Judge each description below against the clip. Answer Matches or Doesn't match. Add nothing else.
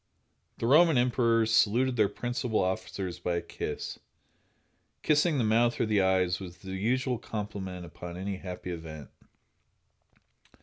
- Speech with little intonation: Doesn't match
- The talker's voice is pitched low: Matches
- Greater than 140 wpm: Doesn't match